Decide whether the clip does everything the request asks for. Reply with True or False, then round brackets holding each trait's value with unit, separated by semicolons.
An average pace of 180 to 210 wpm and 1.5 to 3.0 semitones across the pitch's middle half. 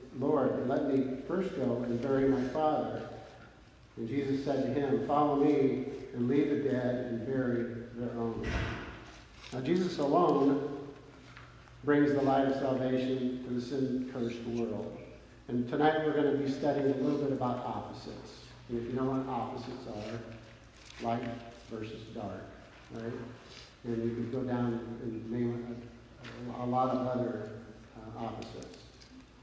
False (150 wpm; 2.6 semitones)